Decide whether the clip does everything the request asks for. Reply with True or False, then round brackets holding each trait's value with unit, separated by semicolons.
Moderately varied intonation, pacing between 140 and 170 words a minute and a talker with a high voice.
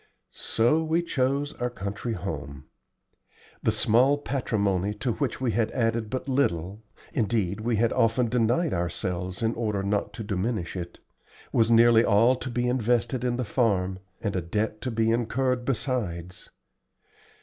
False (3.8 semitones; 150 wpm; 115 Hz)